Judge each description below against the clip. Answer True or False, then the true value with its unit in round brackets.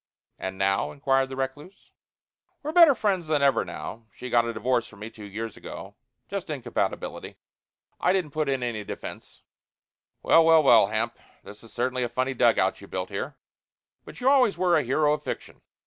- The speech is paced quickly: False (185 wpm)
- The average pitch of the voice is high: False (130 Hz)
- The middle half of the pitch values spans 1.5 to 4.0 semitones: False (5.5 semitones)